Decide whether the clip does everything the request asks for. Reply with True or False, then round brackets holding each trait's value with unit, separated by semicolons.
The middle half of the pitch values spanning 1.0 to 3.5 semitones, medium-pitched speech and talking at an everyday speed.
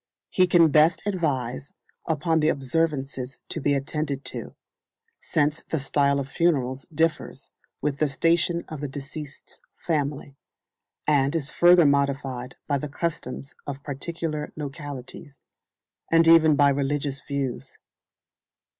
False (2.7 semitones; 145 Hz; 125 wpm)